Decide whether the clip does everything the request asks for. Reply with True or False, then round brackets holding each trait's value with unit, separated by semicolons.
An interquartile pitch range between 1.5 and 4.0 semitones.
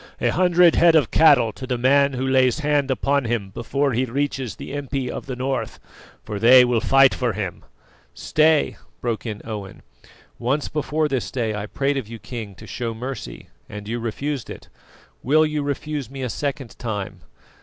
True (3.6 semitones)